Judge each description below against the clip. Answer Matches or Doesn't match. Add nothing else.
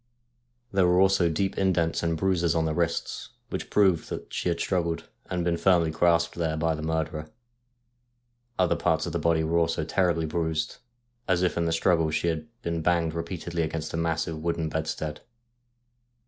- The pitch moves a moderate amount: Doesn't match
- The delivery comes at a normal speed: Matches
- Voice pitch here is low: Matches